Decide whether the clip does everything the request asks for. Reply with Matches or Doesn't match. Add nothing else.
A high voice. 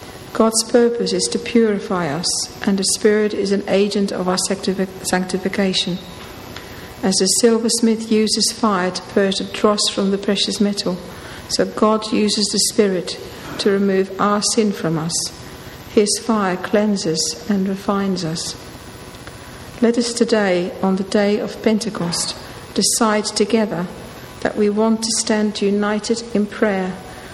Matches